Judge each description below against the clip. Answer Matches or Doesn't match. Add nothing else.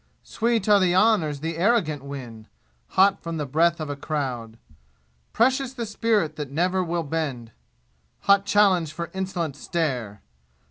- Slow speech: Doesn't match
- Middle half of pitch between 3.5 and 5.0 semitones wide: Doesn't match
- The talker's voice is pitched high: Doesn't match